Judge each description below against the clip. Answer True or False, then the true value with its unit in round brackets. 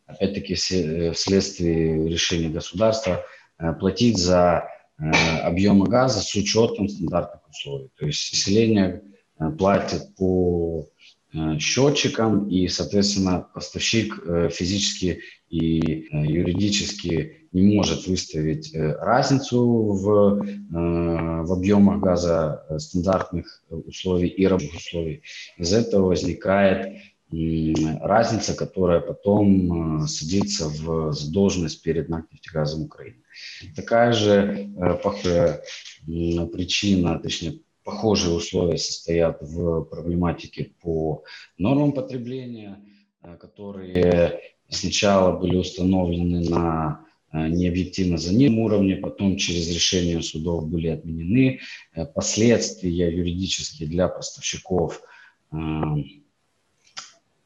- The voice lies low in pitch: True (90 Hz)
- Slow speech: True (90 wpm)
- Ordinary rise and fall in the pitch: True (3.3 semitones)